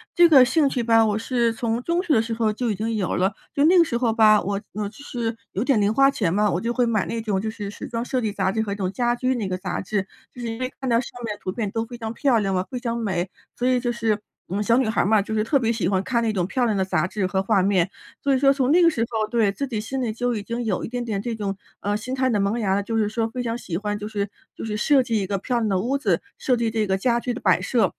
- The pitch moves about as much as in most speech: Yes, average, 3.2 semitones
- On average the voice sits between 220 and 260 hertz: Yes, high, 225 Hz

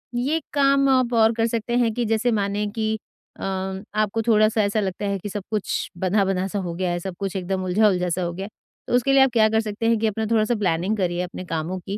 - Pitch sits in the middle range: No, high, 205 Hz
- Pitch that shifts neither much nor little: Yes, average, 3.2 semitones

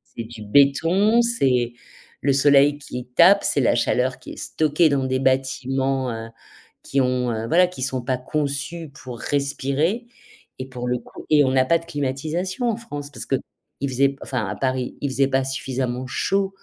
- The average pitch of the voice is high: No, low, 135 Hz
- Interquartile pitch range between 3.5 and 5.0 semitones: No, average, 3.0 semitones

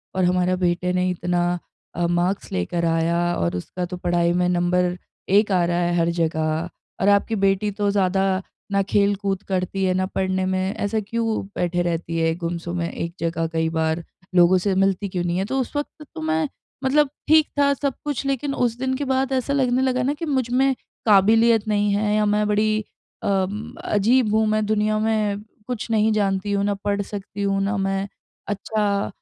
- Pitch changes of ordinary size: Yes, average, 3.5 semitones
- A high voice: Yes, high, 195 Hz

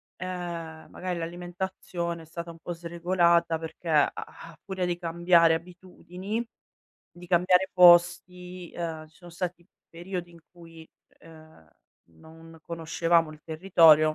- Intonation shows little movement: Yes, narrow, 1.5 semitones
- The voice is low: No, medium, 170 Hz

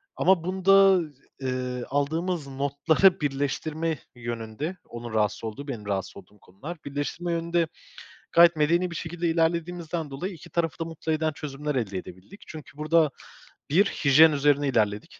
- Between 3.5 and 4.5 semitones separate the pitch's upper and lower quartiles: Yes, average, 4.1 semitones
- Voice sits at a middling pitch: Yes, medium, 150 Hz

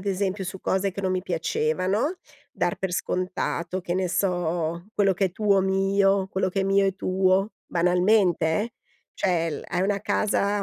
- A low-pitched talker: No, high, 190 Hz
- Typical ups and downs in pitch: No, narrow, 1.8 semitones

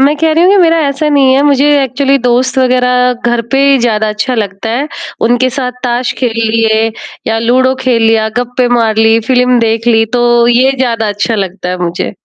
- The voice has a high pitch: Yes, high, 245 Hz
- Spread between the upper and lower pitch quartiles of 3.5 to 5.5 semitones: No, average, 2.7 semitones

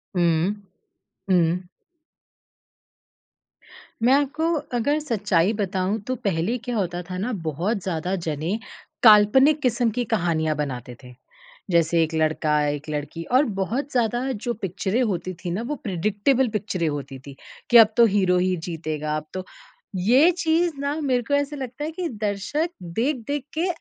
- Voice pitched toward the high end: Yes, high, 205 Hz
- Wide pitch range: Yes, wide, 7.2 semitones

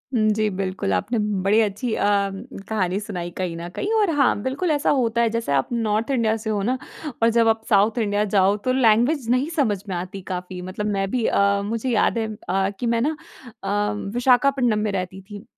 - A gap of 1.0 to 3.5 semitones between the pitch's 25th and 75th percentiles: Yes, average, 3.2 semitones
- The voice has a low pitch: No, high, 215 Hz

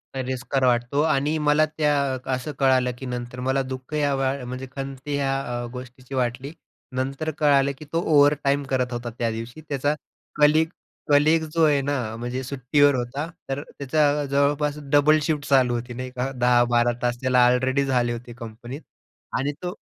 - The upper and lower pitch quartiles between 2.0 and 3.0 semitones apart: Yes, average, 2.7 semitones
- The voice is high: No, low, 135 Hz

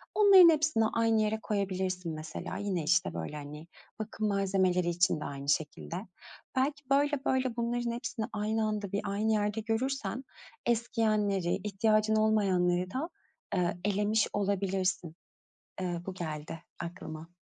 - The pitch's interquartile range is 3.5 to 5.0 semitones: Yes, average, 4.0 semitones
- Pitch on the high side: Yes, high, 205 Hz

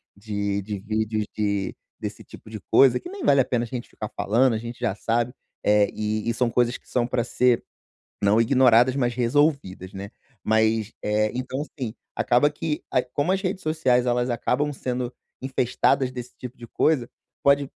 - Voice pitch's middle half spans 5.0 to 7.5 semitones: No, average, 3.1 semitones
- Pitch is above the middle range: No, low, 120 Hz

